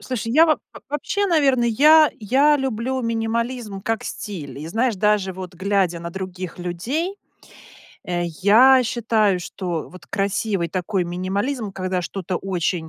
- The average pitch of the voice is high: Yes, high, 205 Hz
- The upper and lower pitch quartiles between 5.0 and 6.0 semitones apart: Yes, wide, 5.5 semitones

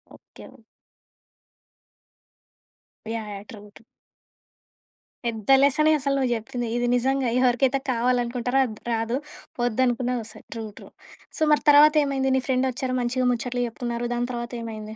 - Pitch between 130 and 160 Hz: No, high, 245 Hz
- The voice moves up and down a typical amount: No, narrow, 2.0 semitones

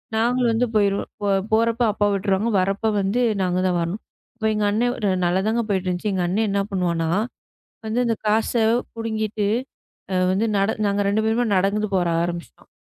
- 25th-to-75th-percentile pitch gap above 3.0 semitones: No, average, 2.7 semitones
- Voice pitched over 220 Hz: No, high, 205 Hz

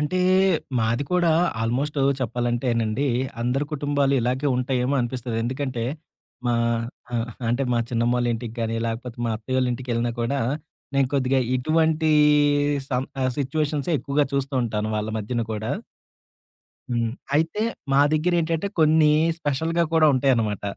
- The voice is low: Yes, low, 130 Hz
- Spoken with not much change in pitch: No, average, 3.6 semitones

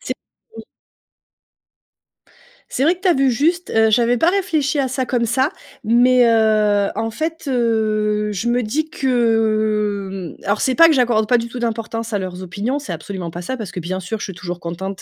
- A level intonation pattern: No, average, 4.1 semitones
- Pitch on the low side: No, high, 225 Hz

